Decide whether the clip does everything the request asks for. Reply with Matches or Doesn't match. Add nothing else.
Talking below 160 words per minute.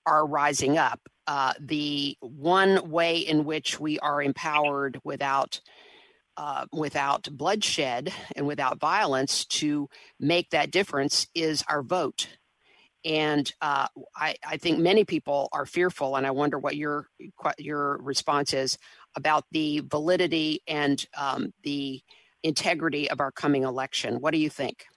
Matches